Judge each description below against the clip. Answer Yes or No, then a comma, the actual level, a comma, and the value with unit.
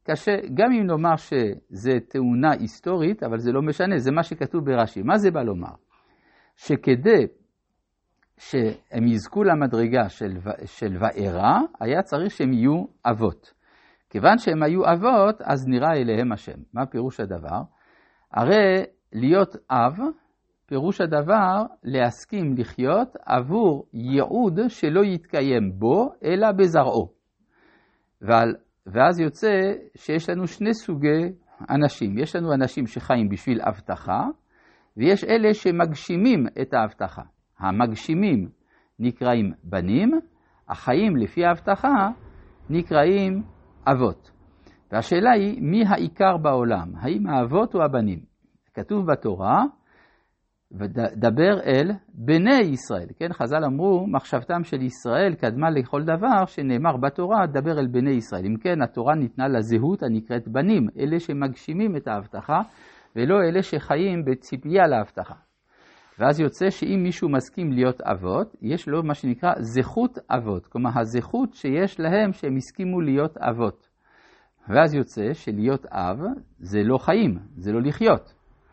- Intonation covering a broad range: Yes, wide, 7.6 semitones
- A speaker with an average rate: Yes, average, 120 wpm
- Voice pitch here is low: No, medium, 150 Hz